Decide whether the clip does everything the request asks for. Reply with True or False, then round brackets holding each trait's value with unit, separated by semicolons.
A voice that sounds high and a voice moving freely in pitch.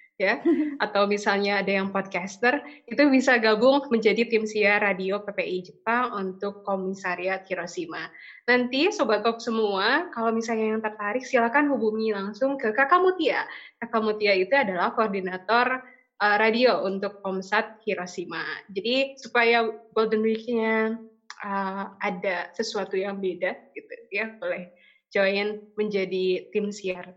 False (215 Hz; 3.1 semitones)